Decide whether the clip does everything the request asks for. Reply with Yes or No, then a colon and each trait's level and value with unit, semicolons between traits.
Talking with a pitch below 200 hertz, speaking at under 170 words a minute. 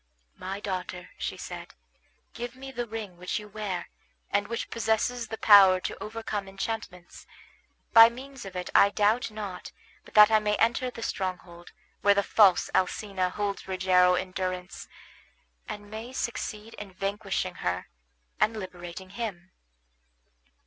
No: high, 205 Hz; average, 145 wpm